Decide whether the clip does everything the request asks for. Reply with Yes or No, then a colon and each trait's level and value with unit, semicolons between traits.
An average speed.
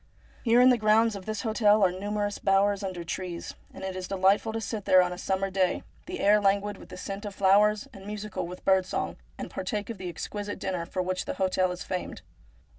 No: fast, 230 wpm